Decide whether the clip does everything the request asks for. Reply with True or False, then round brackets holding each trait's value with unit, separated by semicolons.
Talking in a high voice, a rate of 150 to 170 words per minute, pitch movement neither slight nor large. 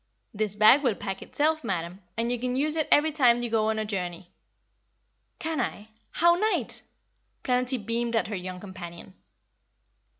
True (230 Hz; 165 wpm; 5.0 semitones)